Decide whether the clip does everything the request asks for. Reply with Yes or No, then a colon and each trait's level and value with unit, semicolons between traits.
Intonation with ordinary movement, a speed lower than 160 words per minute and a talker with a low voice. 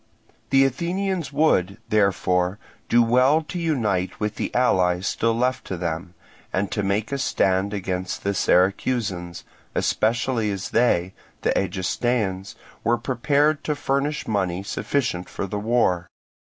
No: wide, 5.7 semitones; slow, 135 wpm; low, 105 Hz